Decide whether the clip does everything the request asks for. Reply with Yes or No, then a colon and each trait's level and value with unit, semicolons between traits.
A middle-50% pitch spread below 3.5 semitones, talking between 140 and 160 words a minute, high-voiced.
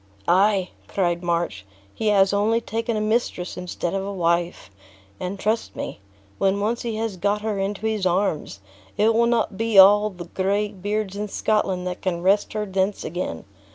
No: average, 2.7 semitones; average, 180 wpm; high, 200 Hz